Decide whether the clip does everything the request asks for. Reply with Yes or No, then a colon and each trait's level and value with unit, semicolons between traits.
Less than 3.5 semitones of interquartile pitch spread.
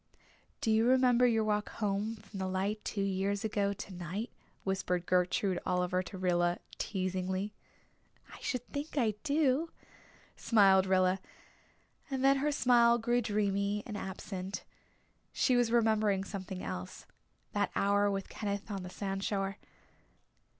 Yes: average, 3.0 semitones